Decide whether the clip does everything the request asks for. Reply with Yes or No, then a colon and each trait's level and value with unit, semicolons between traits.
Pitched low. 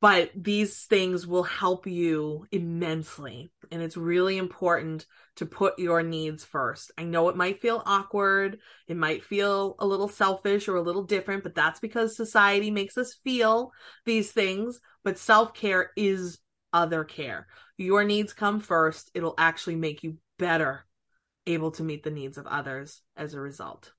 No: medium, 185 Hz